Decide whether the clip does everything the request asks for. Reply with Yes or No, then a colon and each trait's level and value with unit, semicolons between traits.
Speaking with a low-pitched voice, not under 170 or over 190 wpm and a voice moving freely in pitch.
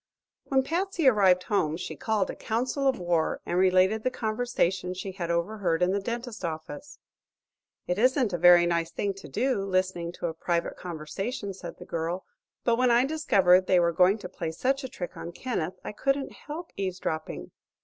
No: high, 190 Hz; average, 185 wpm; wide, 5.9 semitones